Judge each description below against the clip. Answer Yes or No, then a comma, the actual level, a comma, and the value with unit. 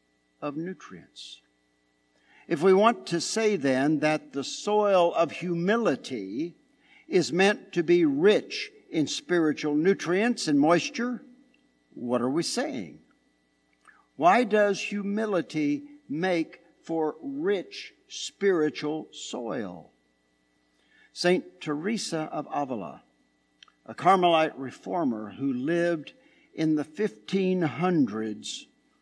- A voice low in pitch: No, medium, 170 Hz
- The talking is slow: Yes, slow, 95 wpm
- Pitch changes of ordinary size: No, wide, 8.1 semitones